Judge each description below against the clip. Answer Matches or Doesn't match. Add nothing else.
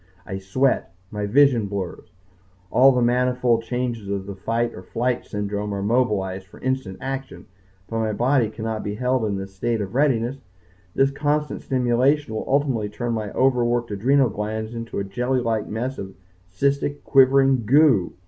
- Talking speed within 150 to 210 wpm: Matches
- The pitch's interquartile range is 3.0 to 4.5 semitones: Matches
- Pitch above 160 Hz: Doesn't match